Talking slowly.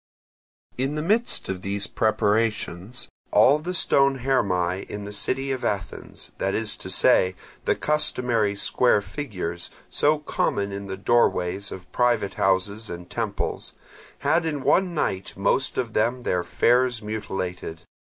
No: average, 145 wpm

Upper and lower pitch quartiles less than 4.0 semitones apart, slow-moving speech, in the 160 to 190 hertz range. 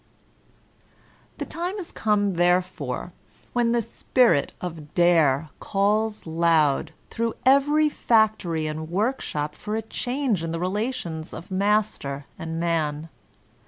No: wide, 5.6 semitones; slow, 125 wpm; medium, 185 Hz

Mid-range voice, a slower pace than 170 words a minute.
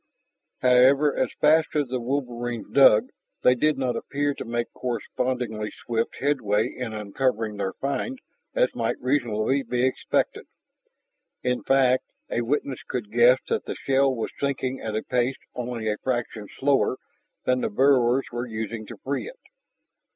No: low, 125 Hz; average, 150 wpm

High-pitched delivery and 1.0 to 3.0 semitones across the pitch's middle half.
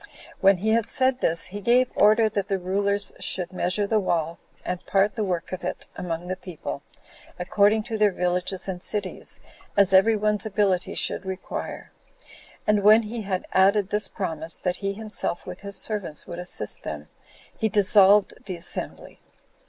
Yes: high, 195 Hz; average, 2.7 semitones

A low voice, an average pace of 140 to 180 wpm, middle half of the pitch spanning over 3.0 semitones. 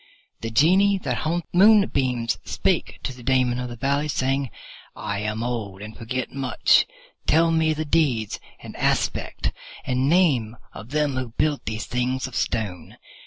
Yes: low, 130 Hz; average, 165 wpm; average, 4.7 semitones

